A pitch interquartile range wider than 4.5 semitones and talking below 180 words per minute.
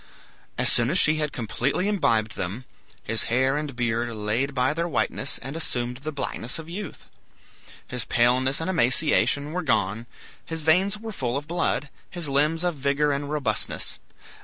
Yes: average, 4.9 semitones; average, 165 wpm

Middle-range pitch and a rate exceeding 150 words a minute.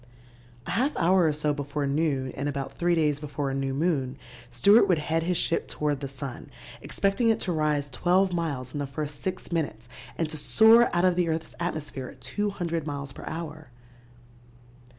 Yes: medium, 155 Hz; average, 190 wpm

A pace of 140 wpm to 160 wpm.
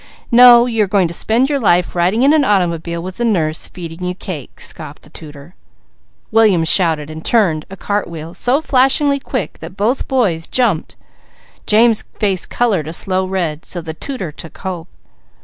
No: average, 180 wpm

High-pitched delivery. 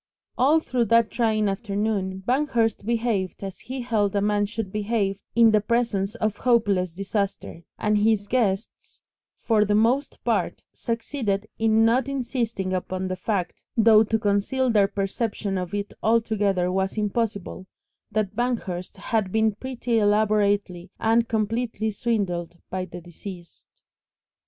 Yes: high, 210 Hz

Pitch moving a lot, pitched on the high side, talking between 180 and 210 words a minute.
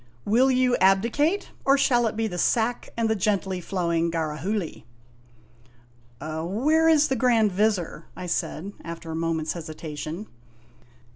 No: wide, 6.1 semitones; high, 195 Hz; average, 145 wpm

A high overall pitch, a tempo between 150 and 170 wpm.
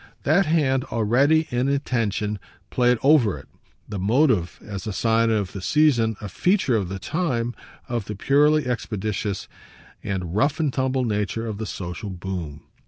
No: low, 115 Hz; average, 160 wpm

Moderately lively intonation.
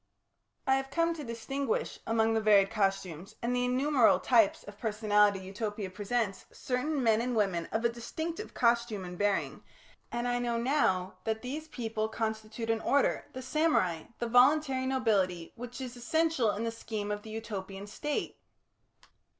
Yes: average, 3.7 semitones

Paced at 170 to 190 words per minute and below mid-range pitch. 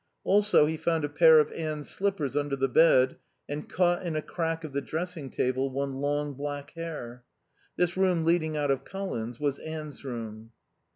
No: average, 180 wpm; medium, 150 Hz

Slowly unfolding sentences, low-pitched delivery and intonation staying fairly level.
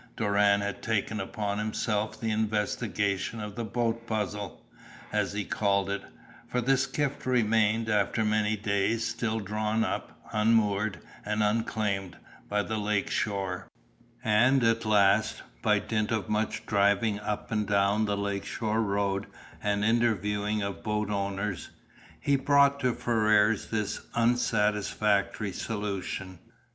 Yes: slow, 130 wpm; low, 105 Hz; narrow, 1.7 semitones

